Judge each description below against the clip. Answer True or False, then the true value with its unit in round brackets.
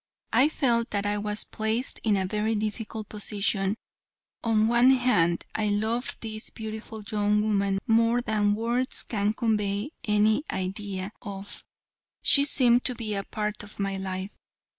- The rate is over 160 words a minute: False (155 wpm)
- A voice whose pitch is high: True (215 Hz)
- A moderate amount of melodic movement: False (2.0 semitones)